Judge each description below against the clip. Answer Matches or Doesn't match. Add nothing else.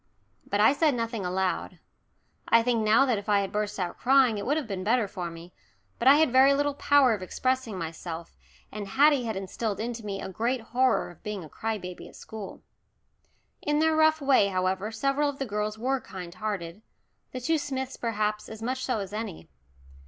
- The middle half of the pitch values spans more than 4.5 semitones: Matches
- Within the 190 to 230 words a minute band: Matches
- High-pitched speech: Matches